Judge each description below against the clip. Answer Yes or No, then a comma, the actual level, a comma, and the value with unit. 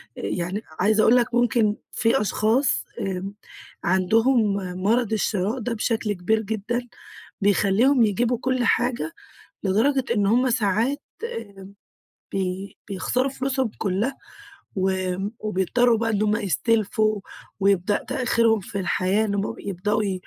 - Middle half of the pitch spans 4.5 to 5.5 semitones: No, average, 3.3 semitones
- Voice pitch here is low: No, high, 215 Hz